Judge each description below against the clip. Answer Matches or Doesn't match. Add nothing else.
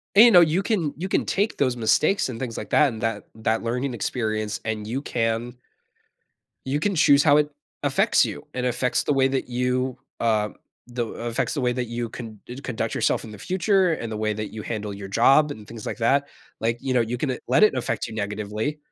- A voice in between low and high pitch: Doesn't match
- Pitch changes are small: Doesn't match